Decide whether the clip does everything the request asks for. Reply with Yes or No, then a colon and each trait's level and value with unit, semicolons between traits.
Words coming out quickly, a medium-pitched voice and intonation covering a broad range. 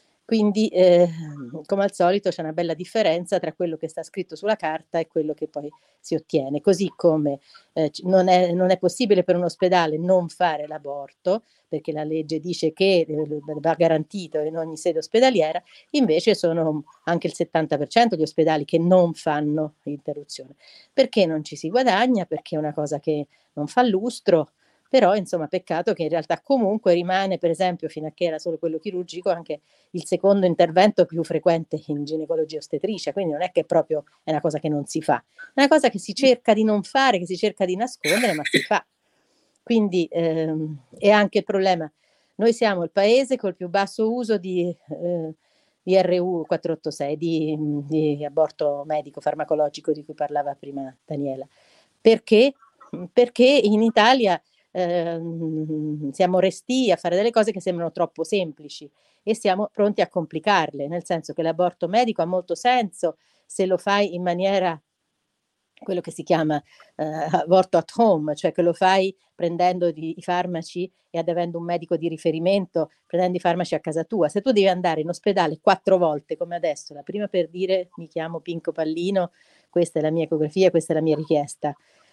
No: fast, 175 wpm; medium, 175 Hz; average, 3.4 semitones